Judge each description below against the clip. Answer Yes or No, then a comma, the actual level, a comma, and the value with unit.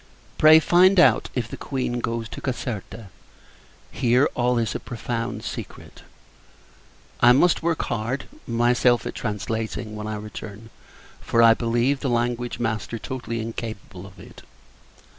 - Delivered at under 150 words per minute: Yes, average, 140 wpm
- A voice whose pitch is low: Yes, low, 120 Hz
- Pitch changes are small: Yes, narrow, 2.0 semitones